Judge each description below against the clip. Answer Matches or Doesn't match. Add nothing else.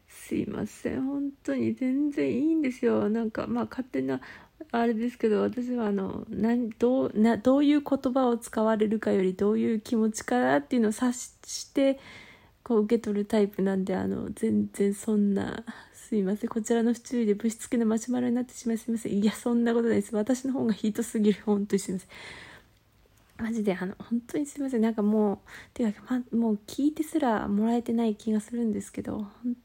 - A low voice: Doesn't match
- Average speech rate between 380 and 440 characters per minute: Matches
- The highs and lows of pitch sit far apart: Doesn't match